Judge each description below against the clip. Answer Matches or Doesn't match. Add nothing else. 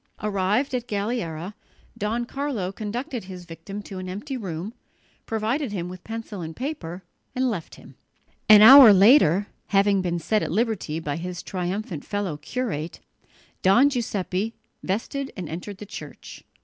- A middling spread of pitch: Matches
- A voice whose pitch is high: Matches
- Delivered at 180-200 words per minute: Doesn't match